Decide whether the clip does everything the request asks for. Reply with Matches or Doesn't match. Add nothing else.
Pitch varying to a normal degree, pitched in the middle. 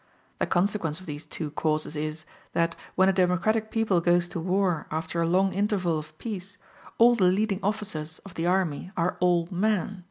Matches